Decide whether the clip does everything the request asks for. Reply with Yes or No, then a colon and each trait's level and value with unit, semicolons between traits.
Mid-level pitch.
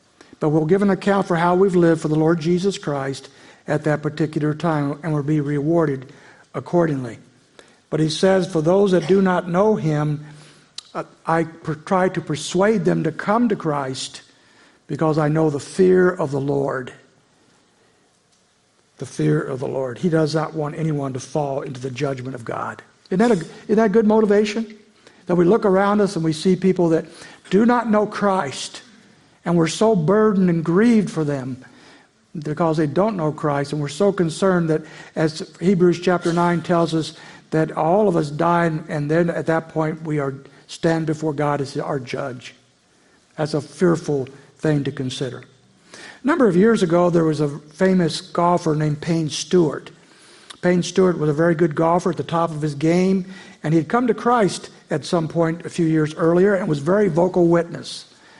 Yes: medium, 165 Hz